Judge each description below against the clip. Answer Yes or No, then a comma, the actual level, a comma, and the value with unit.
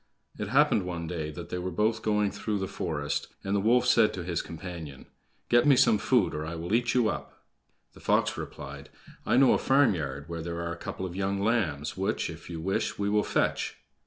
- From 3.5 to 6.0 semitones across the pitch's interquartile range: Yes, average, 4.3 semitones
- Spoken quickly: Yes, fast, 220 wpm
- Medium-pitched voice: No, very low, 95 Hz